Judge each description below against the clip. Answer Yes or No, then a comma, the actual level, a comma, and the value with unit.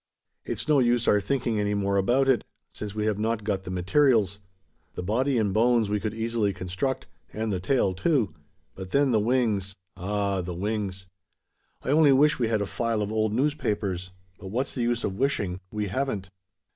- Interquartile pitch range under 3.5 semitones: No, average, 3.8 semitones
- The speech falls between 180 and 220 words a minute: Yes, average, 190 wpm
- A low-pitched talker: Yes, low, 105 Hz